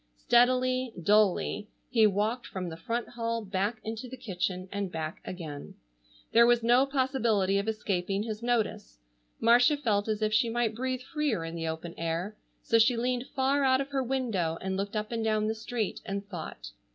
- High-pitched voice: Yes, high, 220 Hz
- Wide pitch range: No, average, 4.2 semitones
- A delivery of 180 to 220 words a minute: Yes, average, 185 wpm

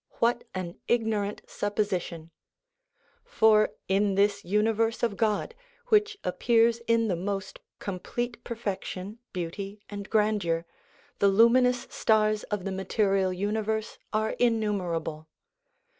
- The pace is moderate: No, slow, 110 wpm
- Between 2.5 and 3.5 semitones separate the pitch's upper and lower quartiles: Yes, average, 2.8 semitones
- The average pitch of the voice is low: No, high, 210 Hz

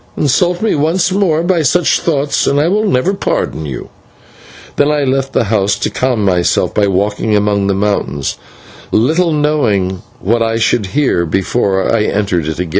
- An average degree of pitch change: No, wide, 7.4 semitones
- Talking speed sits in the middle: Yes, average, 175 wpm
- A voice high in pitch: No, low, 115 Hz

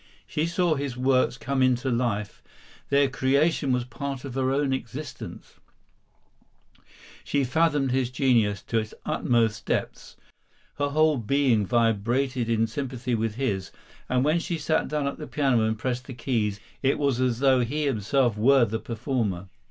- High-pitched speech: No, low, 130 Hz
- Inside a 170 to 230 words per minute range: No, average, 160 wpm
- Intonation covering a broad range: No, average, 3.2 semitones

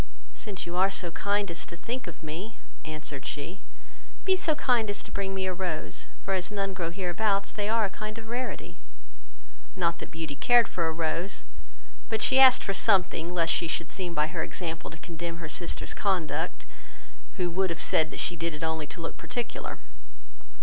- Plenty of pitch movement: No, average, 3.6 semitones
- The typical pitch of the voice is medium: Yes, medium, 180 Hz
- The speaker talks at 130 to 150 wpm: No, average, 195 wpm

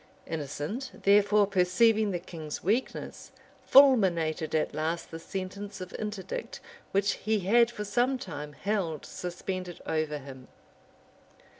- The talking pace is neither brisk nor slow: No, slow, 120 wpm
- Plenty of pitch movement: No, average, 4.7 semitones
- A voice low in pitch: No, medium, 185 Hz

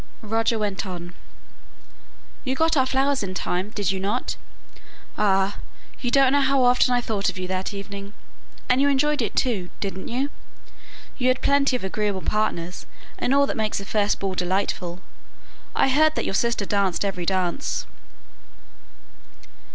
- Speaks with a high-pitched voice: Yes, high, 210 Hz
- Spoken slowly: No, average, 160 wpm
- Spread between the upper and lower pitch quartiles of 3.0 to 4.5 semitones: No, average, 5.2 semitones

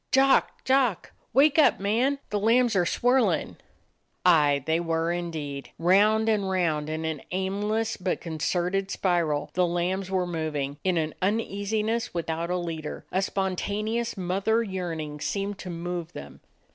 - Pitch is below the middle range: No, medium, 185 Hz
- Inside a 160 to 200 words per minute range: No, average, 145 wpm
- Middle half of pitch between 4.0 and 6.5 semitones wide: Yes, average, 4.3 semitones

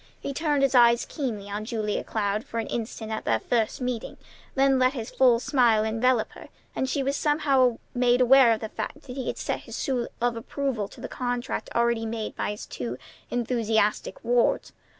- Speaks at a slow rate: No, average, 195 wpm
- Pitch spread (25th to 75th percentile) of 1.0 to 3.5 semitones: Yes, average, 2.9 semitones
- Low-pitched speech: No, high, 240 Hz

